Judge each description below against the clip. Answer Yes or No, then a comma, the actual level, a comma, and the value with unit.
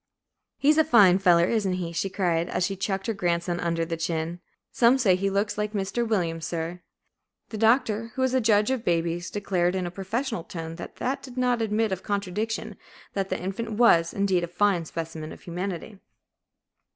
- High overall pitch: Yes, high, 195 Hz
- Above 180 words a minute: Yes, average, 190 wpm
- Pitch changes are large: No, average, 4.2 semitones